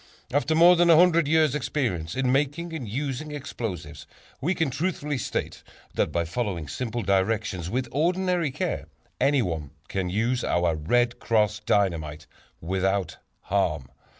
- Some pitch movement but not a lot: No, wide, 8.4 semitones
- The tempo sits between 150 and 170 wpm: No, average, 140 wpm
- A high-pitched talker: No, low, 120 Hz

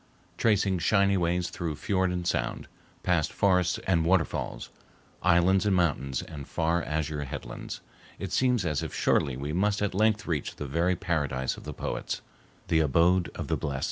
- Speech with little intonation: No, average, 3.7 semitones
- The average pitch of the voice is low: Yes, very low, 85 Hz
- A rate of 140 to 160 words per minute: No, average, 170 wpm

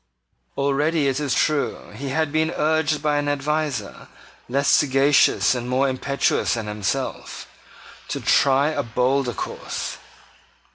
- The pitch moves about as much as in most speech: No, narrow, 2.3 semitones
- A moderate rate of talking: No, slow, 130 wpm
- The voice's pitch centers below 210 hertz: Yes, medium, 140 Hz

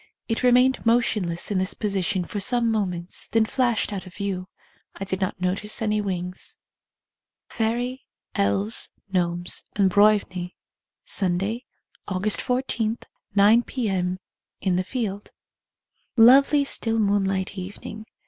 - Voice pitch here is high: Yes, high, 205 Hz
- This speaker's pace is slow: Yes, slow, 125 wpm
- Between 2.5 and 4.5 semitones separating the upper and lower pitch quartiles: Yes, average, 3.6 semitones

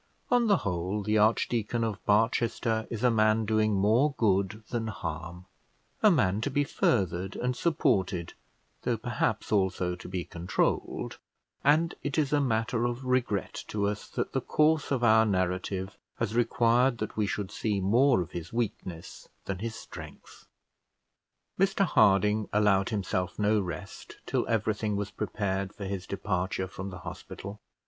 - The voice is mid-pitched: No, low, 105 Hz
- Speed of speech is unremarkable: Yes, average, 155 wpm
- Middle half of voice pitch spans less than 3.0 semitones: No, average, 3.7 semitones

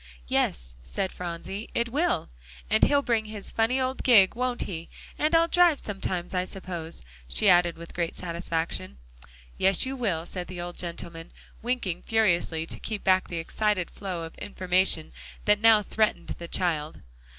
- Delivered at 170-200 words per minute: No, average, 160 wpm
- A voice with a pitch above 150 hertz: Yes, medium, 185 Hz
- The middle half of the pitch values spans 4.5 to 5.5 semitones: Yes, average, 4.8 semitones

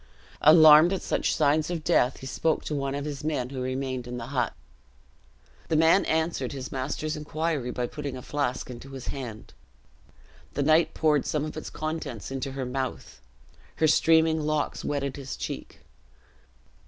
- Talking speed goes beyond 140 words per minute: Yes, average, 165 wpm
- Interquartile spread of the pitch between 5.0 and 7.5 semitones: No, average, 3.2 semitones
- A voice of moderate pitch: Yes, medium, 145 Hz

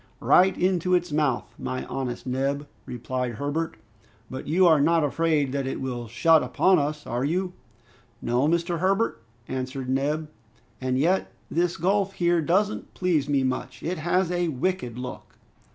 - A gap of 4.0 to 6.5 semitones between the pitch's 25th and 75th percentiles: Yes, average, 5.1 semitones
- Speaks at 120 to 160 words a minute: Yes, average, 155 wpm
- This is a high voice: No, medium, 150 Hz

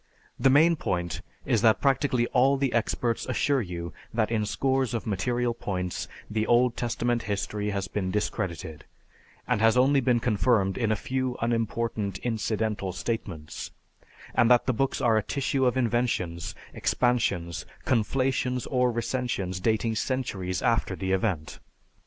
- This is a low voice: Yes, low, 115 Hz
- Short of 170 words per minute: Yes, average, 145 wpm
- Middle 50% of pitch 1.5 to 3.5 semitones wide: No, average, 4.1 semitones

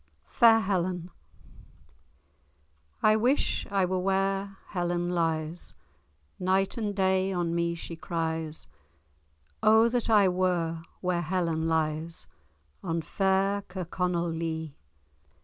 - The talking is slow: Yes, slow, 105 wpm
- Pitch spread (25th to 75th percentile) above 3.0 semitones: No, average, 2.7 semitones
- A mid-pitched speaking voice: Yes, medium, 180 Hz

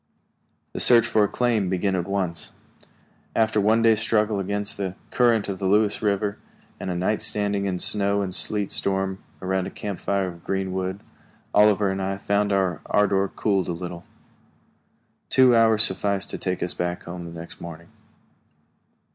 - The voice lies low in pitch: Yes, low, 100 Hz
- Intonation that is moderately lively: No, narrow, 2.1 semitones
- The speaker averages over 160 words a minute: Yes, average, 170 wpm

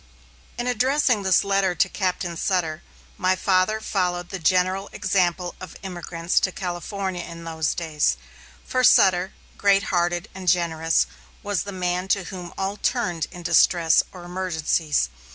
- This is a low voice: No, medium, 180 Hz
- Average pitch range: No, narrow, 2.0 semitones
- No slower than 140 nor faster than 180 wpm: Yes, average, 145 wpm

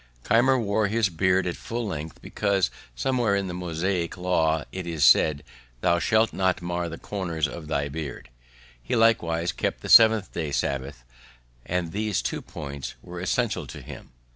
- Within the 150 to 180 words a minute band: Yes, average, 165 wpm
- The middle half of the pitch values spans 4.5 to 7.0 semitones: No, average, 4.1 semitones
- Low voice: Yes, very low, 90 Hz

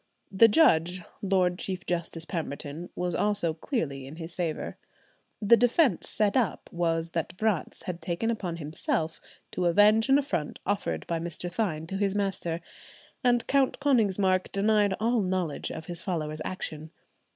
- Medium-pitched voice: Yes, medium, 180 Hz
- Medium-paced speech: Yes, average, 150 wpm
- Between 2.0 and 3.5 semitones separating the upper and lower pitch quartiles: No, average, 4.1 semitones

